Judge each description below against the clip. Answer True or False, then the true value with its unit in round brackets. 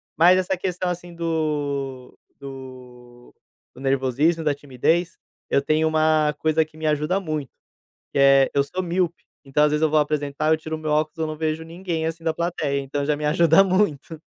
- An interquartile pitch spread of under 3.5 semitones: True (2.8 semitones)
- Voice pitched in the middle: True (155 Hz)